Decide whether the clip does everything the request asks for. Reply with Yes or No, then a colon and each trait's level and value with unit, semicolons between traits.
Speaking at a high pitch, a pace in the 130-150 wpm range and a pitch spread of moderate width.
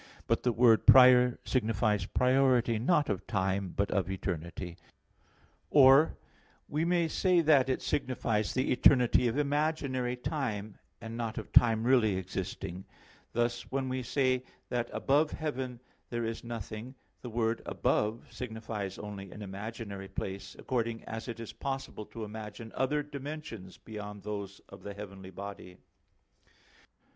No: low, 115 Hz; average, 140 wpm; average, 4.1 semitones